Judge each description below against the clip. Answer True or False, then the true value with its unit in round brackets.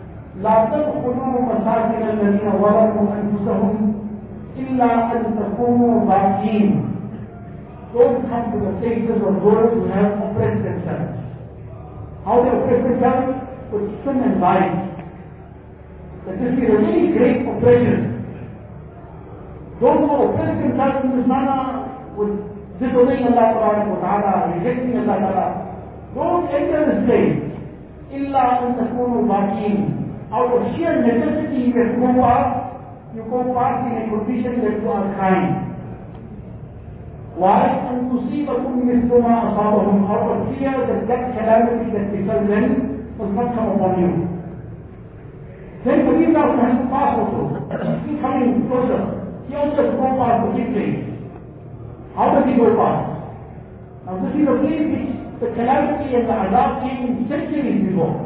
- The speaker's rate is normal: False (130 wpm)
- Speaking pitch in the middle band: False (235 Hz)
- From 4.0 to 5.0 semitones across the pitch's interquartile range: False (3.5 semitones)